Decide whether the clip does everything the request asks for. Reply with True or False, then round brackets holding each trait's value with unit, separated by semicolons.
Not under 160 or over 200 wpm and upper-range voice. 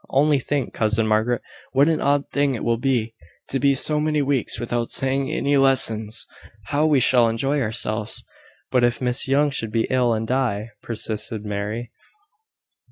False (165 wpm; 125 Hz)